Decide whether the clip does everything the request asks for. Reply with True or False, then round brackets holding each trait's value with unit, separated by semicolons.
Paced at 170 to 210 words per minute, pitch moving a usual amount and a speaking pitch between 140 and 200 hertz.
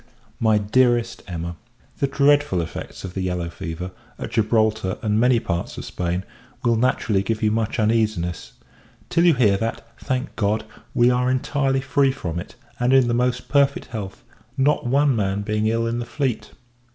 False (175 wpm; 4.3 semitones; 115 Hz)